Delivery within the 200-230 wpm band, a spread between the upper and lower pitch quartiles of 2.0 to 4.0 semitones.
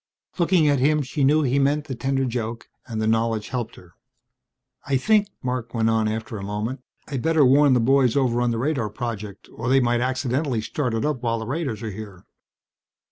Yes: fast, 205 wpm; average, 3.6 semitones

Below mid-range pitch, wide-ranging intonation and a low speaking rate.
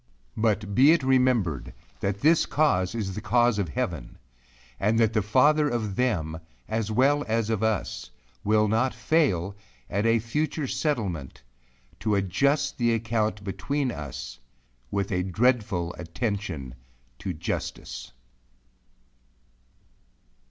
No: low, 110 Hz; average, 5.0 semitones; slow, 125 wpm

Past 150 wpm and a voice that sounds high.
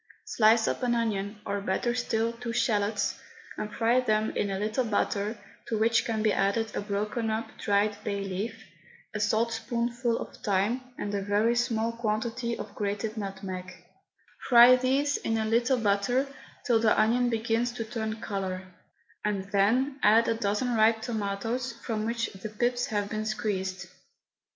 Yes: average, 160 wpm; high, 220 Hz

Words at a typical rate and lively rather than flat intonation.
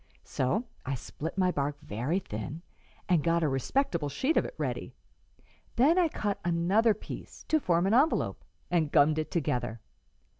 Yes: average, 160 wpm; wide, 6.6 semitones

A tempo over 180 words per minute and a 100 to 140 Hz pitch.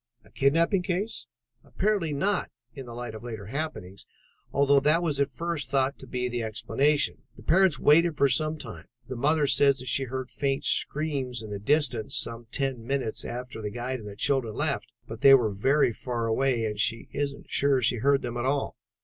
Yes: average, 200 wpm; low, 135 Hz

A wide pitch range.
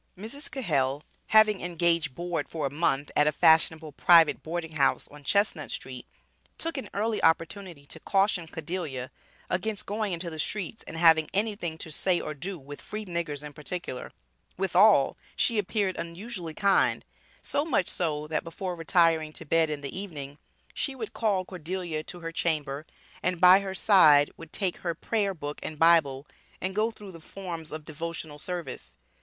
No: average, 4.0 semitones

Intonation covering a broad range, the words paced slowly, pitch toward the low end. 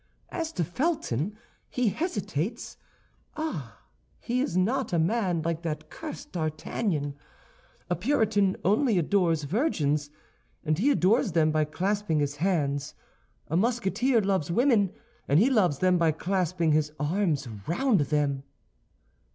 No: wide, 6.2 semitones; slow, 130 wpm; medium, 180 Hz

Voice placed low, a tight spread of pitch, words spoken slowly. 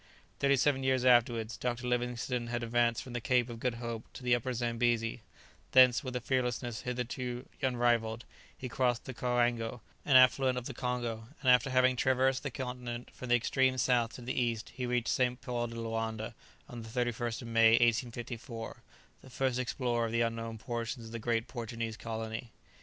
No: low, 120 Hz; narrow, 1.5 semitones; average, 185 wpm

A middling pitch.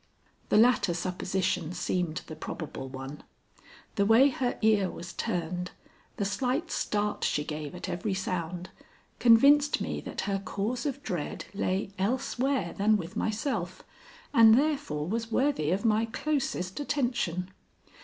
No: high, 200 Hz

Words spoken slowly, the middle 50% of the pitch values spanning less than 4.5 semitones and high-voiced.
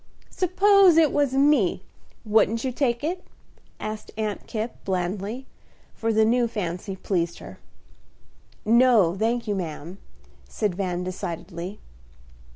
No: slow, 120 wpm; average, 5.2 semitones; high, 215 Hz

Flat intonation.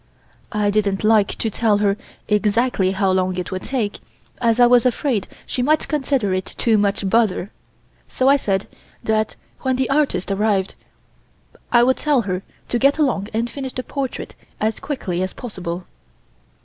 No: average, 4.4 semitones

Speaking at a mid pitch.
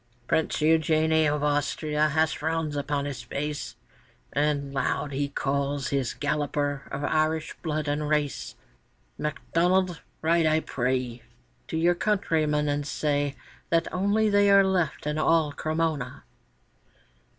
Yes: medium, 150 Hz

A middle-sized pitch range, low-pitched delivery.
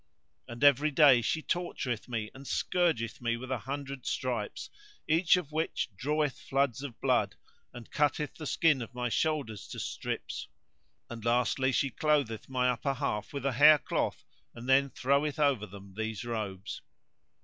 Yes: average, 3.7 semitones; low, 130 Hz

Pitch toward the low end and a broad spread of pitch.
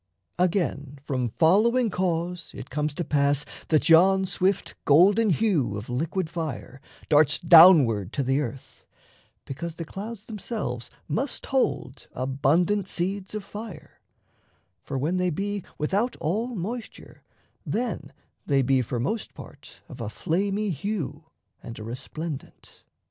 No: medium, 165 Hz; wide, 6.1 semitones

